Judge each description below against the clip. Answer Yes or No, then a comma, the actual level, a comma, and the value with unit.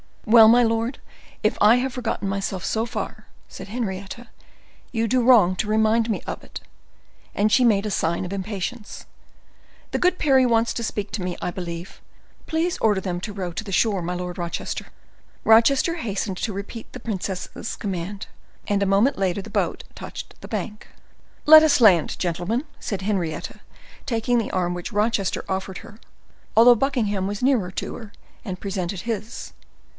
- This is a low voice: No, high, 210 Hz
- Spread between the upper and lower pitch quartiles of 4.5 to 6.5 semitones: No, average, 3.6 semitones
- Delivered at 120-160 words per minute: No, average, 175 wpm